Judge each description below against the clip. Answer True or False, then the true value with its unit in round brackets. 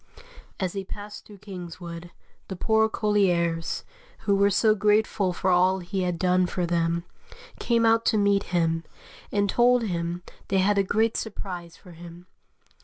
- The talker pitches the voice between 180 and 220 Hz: True (190 Hz)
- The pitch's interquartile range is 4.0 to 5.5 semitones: False (3.1 semitones)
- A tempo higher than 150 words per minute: True (160 wpm)